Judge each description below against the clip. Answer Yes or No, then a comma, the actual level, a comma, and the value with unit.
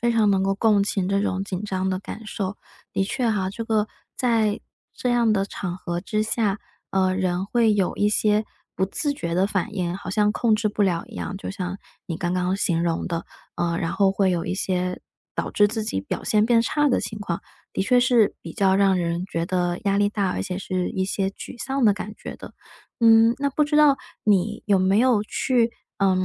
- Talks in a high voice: Yes, high, 200 Hz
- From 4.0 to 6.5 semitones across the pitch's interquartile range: No, average, 2.9 semitones